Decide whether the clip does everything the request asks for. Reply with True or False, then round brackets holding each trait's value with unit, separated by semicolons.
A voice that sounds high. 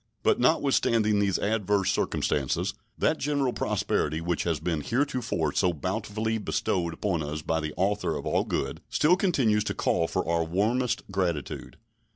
False (100 Hz)